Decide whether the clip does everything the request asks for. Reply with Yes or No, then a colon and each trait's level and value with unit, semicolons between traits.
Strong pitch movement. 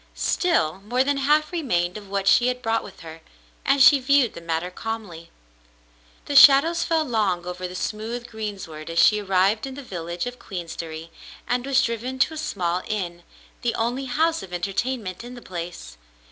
Yes: wide, 6.7 semitones